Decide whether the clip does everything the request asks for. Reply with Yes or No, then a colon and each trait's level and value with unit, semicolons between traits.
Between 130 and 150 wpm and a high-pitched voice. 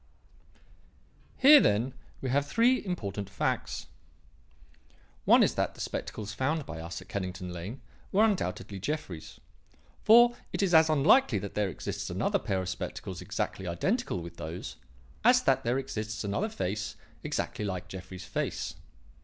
No: average, 145 wpm; low, 105 Hz